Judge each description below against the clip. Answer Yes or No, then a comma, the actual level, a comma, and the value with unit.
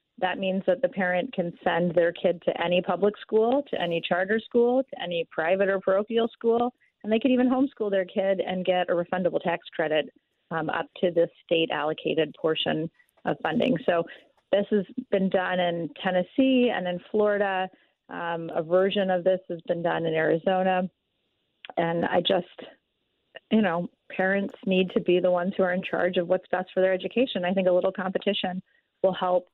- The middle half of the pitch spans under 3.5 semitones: Yes, average, 2.9 semitones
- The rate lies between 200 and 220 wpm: No, average, 190 wpm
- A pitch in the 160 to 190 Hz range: Yes, medium, 185 Hz